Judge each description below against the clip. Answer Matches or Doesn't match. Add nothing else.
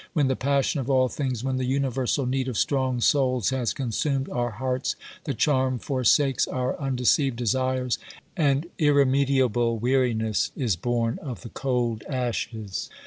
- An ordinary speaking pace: Matches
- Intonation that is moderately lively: Doesn't match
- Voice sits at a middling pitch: Doesn't match